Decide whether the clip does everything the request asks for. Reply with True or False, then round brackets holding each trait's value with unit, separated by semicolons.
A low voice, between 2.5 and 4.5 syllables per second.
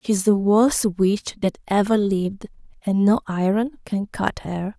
False (205 Hz; 4.3 syllables/s)